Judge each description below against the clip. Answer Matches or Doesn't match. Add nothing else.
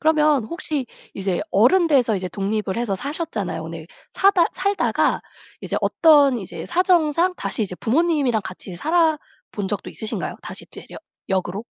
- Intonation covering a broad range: Matches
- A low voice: Doesn't match